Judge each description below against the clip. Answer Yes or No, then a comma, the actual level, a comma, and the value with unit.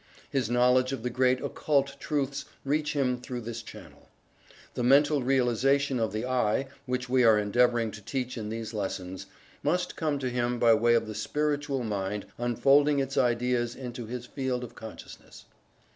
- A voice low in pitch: Yes, low, 125 Hz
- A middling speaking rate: Yes, average, 170 wpm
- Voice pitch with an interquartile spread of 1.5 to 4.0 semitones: Yes, average, 2.8 semitones